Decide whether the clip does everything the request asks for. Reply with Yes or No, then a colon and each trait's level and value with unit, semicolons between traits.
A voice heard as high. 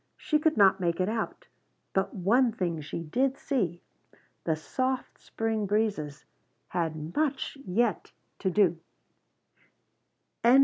Yes: high, 195 Hz